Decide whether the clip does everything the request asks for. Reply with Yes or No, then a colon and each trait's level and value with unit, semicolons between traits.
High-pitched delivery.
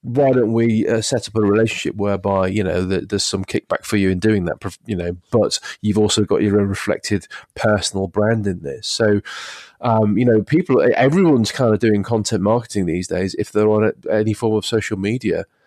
No: low, 105 Hz